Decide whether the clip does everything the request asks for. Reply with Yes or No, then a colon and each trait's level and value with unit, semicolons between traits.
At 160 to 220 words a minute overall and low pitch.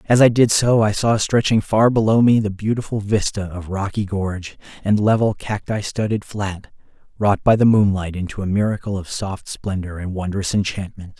Yes: average, 180 wpm; low, 100 Hz